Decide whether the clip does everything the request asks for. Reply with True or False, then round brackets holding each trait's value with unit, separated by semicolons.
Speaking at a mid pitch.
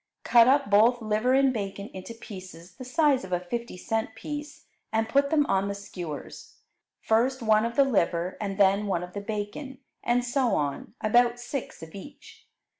False (220 Hz)